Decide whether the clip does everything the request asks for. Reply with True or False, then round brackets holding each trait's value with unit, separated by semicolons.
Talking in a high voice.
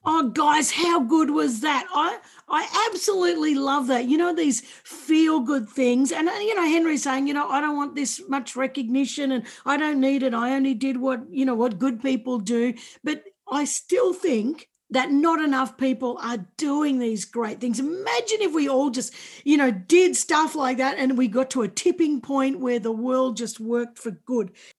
True (270 Hz)